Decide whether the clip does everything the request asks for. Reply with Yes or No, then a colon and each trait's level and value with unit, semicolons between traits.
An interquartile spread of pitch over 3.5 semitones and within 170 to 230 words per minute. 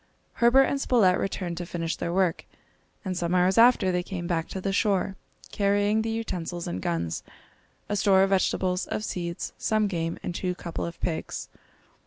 No: average, 3.0 semitones; average, 180 wpm